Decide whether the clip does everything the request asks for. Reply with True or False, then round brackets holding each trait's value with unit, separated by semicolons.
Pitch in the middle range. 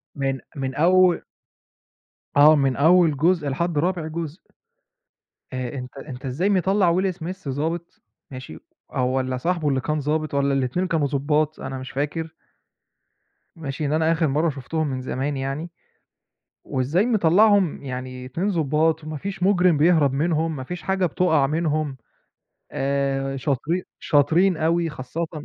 True (155 Hz)